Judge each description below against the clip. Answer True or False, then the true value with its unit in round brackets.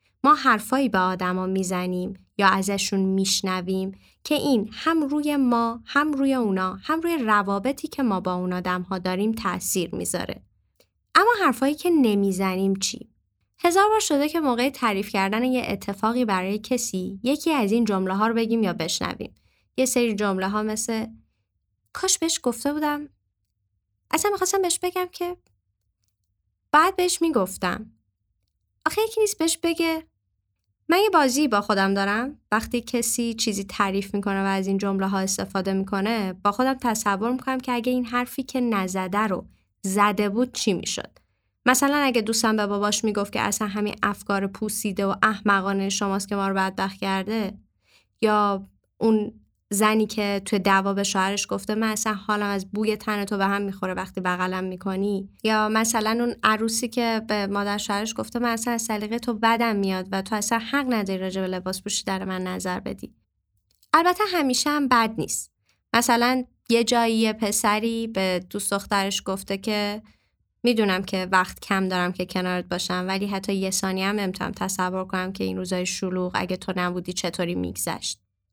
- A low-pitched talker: False (205 Hz)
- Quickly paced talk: True (165 wpm)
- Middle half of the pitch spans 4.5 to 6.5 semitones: False (4.1 semitones)